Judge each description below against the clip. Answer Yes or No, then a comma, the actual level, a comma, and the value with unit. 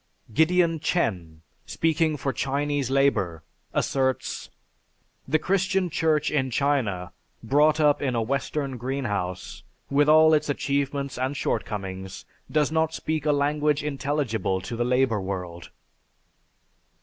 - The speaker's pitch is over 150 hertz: No, medium, 140 Hz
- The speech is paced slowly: Yes, slow, 120 wpm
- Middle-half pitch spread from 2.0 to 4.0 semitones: No, average, 4.9 semitones